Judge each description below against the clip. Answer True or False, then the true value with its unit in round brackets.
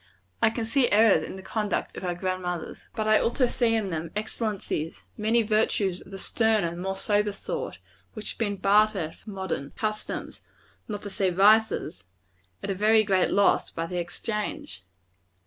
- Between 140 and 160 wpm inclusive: False (175 wpm)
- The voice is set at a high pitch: True (205 Hz)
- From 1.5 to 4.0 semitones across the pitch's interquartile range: True (2.8 semitones)